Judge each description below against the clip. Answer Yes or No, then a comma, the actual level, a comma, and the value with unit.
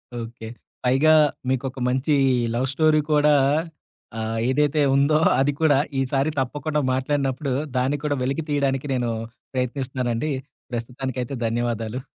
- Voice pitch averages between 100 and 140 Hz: Yes, low, 135 Hz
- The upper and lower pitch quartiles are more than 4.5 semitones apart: No, average, 2.7 semitones